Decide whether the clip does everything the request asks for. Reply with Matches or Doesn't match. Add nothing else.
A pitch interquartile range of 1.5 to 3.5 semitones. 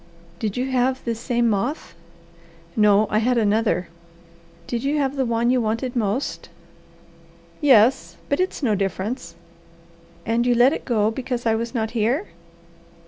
Matches